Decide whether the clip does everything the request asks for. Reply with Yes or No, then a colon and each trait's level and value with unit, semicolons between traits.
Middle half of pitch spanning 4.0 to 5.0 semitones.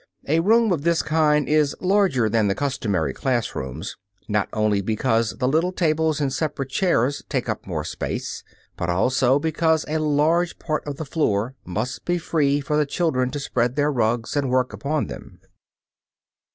No: wide, 5.4 semitones